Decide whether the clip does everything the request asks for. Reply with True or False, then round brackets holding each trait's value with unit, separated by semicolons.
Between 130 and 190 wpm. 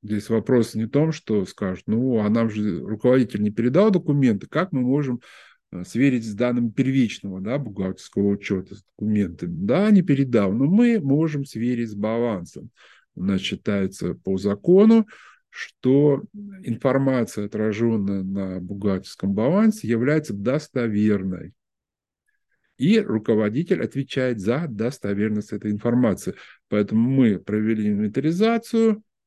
False (120 wpm)